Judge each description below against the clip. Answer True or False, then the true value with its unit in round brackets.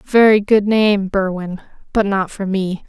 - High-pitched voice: True (200 Hz)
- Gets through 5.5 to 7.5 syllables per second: False (4.5 syllables/s)